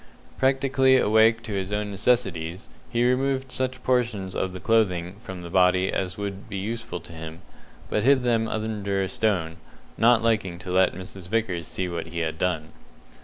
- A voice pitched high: No, low, 100 Hz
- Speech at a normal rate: Yes, average, 170 wpm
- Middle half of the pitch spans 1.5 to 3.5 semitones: No, average, 4.2 semitones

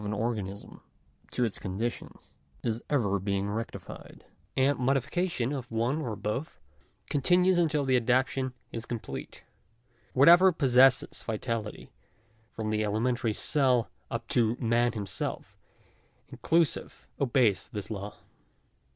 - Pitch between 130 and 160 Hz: No, low, 120 Hz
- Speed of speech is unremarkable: No, slow, 120 wpm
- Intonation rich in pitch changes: No, average, 3.8 semitones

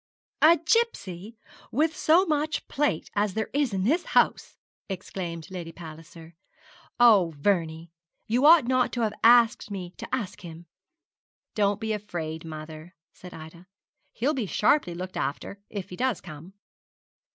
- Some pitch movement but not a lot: No, wide, 6.4 semitones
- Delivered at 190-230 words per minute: No, average, 150 wpm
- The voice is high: Yes, high, 200 Hz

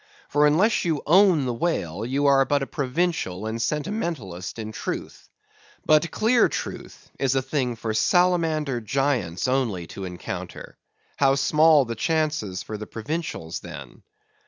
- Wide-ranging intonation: Yes, wide, 6.2 semitones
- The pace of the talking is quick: No, average, 145 wpm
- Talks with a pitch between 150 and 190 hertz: No, low, 135 Hz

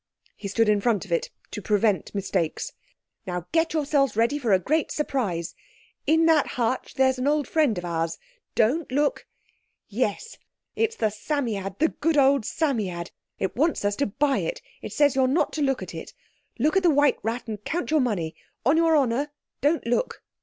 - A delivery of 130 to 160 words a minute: No, average, 180 wpm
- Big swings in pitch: Yes, wide, 6.5 semitones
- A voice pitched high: Yes, very high, 260 Hz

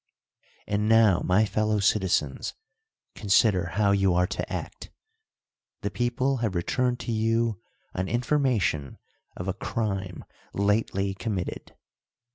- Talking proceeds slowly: Yes, slow, 115 wpm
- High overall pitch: No, low, 105 Hz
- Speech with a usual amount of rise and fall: Yes, average, 3.2 semitones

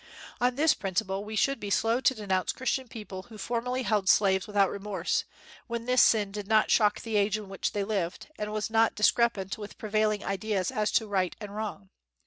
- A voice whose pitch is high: Yes, high, 210 Hz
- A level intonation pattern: Yes, narrow, 2.3 semitones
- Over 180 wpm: Yes, average, 200 wpm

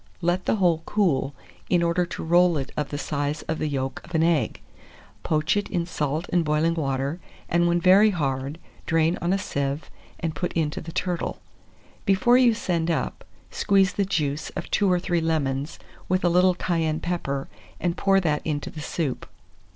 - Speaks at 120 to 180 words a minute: No, average, 190 wpm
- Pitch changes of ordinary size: Yes, average, 3.1 semitones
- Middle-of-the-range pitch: Yes, medium, 165 Hz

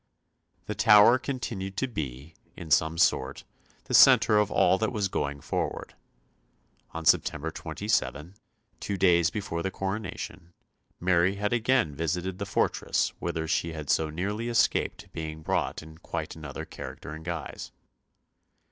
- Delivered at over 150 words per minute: No, average, 140 wpm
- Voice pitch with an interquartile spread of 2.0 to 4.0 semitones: No, average, 4.5 semitones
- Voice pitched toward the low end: Yes, very low, 85 Hz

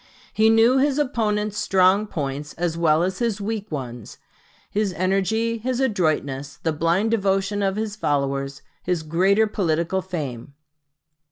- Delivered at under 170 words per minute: Yes, average, 140 wpm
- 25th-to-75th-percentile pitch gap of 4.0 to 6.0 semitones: Yes, wide, 5.5 semitones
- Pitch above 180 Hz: Yes, high, 190 Hz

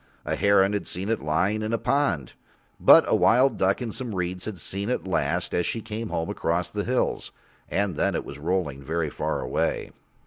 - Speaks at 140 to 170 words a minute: No, fast, 205 wpm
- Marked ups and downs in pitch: No, average, 4.0 semitones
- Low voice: Yes, very low, 95 Hz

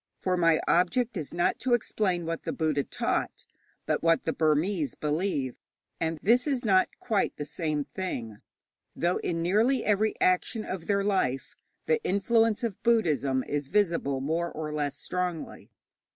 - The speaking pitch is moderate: Yes, medium, 175 Hz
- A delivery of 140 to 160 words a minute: Yes, average, 155 wpm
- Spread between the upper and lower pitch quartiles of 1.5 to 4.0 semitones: No, wide, 5.4 semitones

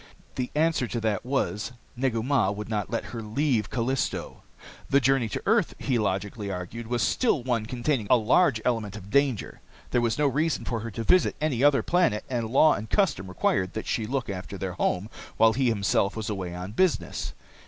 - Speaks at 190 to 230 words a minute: Yes, average, 195 wpm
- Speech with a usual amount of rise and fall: Yes, average, 4.3 semitones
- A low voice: Yes, low, 115 Hz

